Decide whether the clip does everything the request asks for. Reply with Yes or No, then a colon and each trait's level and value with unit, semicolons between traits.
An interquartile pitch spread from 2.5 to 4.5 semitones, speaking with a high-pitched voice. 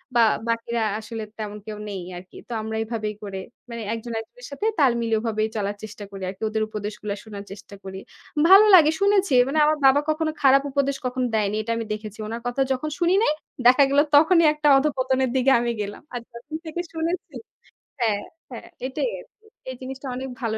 No: average, 5.2 semitones; high, 240 Hz